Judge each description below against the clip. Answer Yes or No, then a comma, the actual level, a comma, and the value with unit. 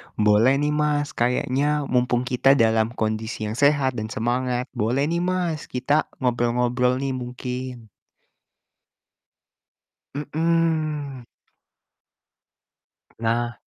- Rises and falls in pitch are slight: No, average, 3.4 semitones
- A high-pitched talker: No, low, 125 Hz